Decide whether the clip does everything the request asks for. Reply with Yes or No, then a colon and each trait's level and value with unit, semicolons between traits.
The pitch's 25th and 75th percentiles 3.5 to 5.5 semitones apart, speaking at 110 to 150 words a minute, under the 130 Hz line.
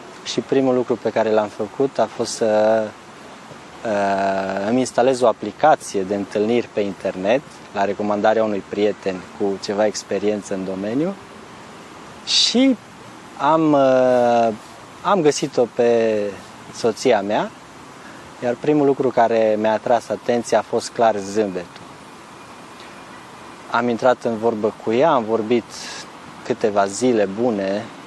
No: average, 3.0 semitones; average, 120 wpm; low, 110 Hz